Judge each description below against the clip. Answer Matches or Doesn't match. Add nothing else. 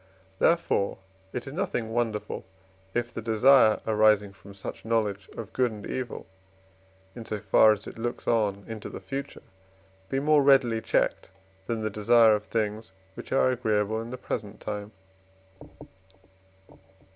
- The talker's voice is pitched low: Matches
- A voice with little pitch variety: Matches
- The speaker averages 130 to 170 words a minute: Matches